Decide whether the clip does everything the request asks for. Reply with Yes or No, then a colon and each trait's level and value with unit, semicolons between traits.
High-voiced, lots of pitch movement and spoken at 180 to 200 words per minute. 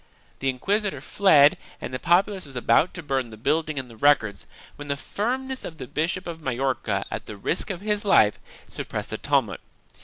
No: medium, 150 Hz; wide, 6.8 semitones; average, 190 wpm